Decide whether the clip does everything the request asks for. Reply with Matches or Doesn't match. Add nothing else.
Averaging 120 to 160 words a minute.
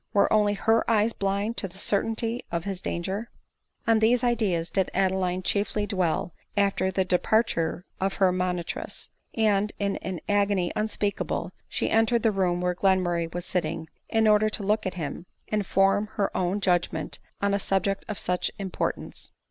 Doesn't match